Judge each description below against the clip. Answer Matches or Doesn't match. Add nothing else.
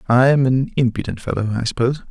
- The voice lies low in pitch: Matches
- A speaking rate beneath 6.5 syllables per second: Doesn't match